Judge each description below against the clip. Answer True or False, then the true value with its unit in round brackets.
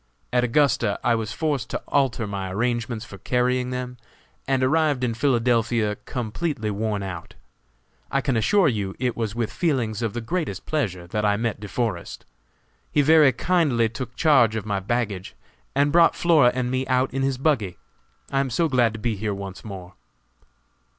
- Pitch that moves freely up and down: False (4.0 semitones)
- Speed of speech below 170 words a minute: False (175 wpm)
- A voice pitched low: True (120 Hz)